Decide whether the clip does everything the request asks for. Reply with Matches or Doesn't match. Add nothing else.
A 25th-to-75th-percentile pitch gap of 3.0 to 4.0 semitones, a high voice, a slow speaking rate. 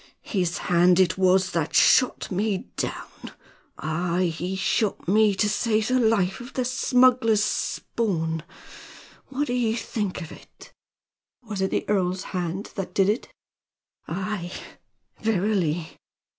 Matches